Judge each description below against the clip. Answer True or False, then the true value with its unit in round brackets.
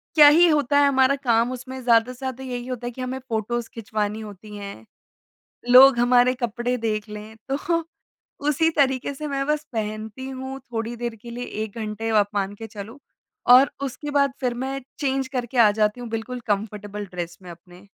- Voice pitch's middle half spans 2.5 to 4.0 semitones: True (3.6 semitones)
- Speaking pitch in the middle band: False (245 Hz)